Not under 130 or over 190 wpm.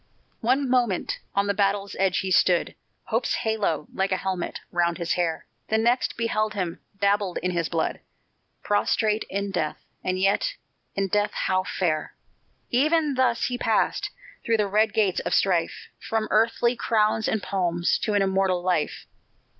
Yes: average, 160 wpm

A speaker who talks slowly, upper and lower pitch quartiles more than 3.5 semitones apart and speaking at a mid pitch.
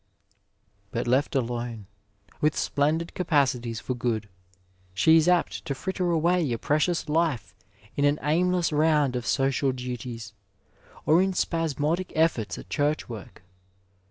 Yes: slow, 130 wpm; average, 5.1 semitones; medium, 145 Hz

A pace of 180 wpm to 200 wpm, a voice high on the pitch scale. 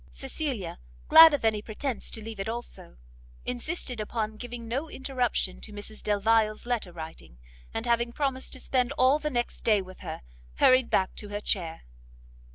No: average, 165 wpm; high, 230 Hz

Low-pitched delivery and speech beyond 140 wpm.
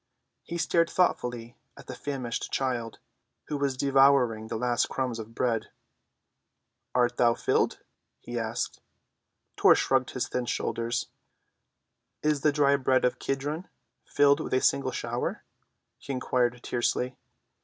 No: low, 125 Hz; slow, 135 wpm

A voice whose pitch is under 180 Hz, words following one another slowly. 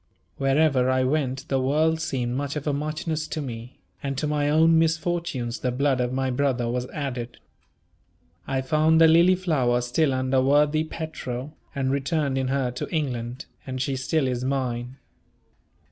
No: low, 135 Hz; average, 160 wpm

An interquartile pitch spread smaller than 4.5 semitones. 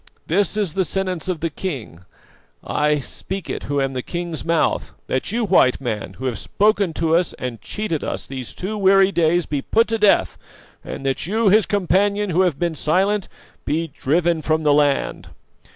No: average, 5.2 semitones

